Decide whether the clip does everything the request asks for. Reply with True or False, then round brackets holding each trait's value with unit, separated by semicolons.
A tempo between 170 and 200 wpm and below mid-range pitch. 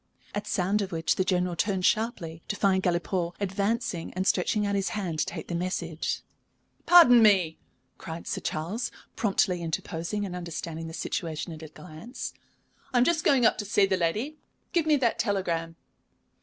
False (175 wpm; 185 Hz)